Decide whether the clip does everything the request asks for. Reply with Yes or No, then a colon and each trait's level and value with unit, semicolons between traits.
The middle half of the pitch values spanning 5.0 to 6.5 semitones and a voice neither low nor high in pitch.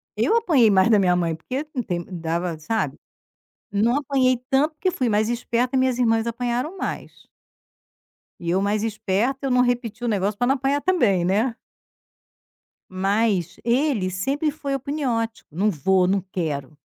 No: wide, 5.5 semitones; high, 225 Hz